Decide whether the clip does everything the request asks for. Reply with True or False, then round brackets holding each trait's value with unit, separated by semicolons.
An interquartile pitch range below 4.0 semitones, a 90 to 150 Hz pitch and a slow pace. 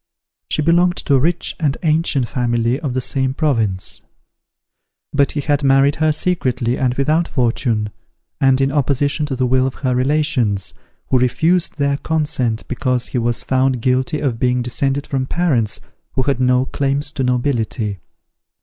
False (2.8 semitones; 135 Hz; 160 wpm)